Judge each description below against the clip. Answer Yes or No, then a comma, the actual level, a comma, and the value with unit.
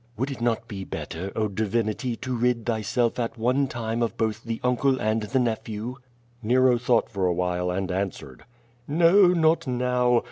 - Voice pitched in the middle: No, low, 115 Hz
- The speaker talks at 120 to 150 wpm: No, average, 175 wpm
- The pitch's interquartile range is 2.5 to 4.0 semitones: Yes, average, 2.8 semitones